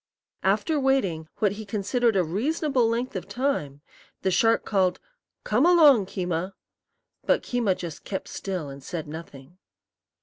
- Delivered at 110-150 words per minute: Yes, average, 140 wpm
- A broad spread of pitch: Yes, wide, 6.1 semitones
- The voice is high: Yes, high, 200 Hz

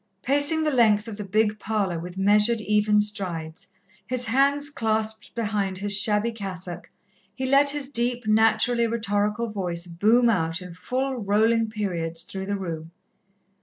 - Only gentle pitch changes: No, average, 3.4 semitones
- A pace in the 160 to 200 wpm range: No, average, 150 wpm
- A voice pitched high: Yes, high, 210 Hz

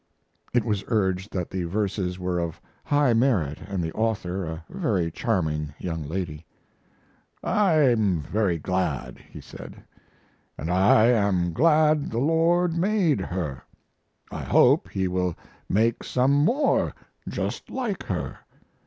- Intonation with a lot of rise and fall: Yes, wide, 7.5 semitones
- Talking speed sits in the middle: No, slow, 130 wpm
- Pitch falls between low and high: No, low, 100 Hz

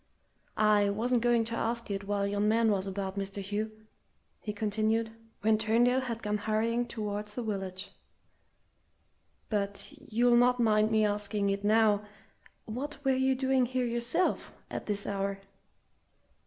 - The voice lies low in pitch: No, high, 215 Hz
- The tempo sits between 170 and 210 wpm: No, average, 145 wpm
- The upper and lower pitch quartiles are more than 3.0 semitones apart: No, narrow, 2.6 semitones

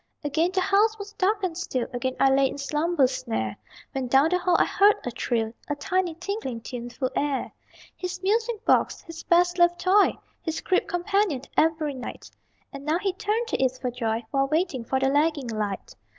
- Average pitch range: No, wide, 6.1 semitones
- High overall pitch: Yes, very high, 315 Hz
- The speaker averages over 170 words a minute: Yes, average, 195 wpm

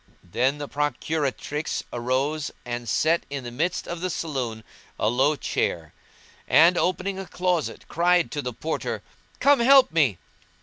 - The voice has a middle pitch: Yes, medium, 150 Hz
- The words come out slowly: No, average, 145 wpm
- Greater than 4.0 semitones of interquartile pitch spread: Yes, wide, 5.5 semitones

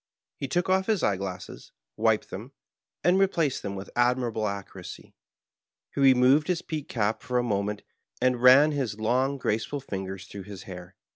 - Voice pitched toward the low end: Yes, low, 125 Hz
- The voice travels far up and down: Yes, wide, 5.9 semitones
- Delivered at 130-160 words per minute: No, average, 170 wpm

